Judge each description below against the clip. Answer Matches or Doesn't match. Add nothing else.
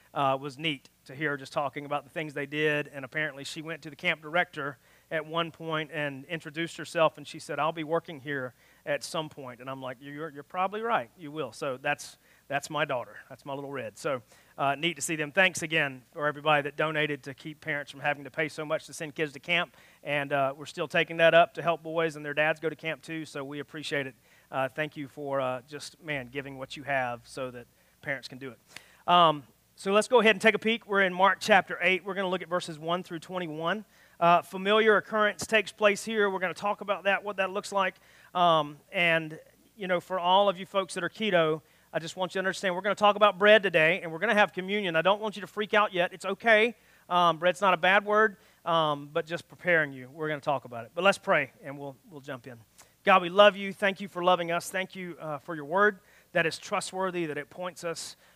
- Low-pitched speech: Doesn't match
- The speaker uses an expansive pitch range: Doesn't match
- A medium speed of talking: Doesn't match